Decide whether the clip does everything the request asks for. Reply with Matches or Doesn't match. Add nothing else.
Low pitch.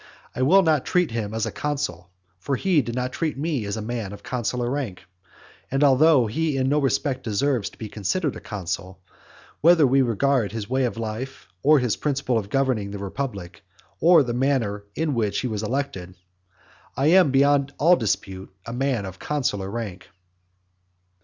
Matches